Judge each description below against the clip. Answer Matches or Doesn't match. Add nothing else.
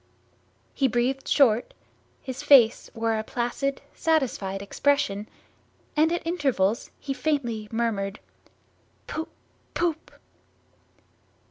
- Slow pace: Matches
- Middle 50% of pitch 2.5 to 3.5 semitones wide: Doesn't match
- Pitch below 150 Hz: Doesn't match